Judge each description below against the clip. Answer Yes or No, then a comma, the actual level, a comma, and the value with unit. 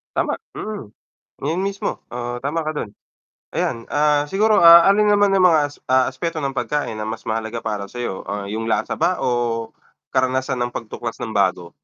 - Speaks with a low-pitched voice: Yes, low, 130 Hz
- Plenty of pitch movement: Yes, wide, 6.7 semitones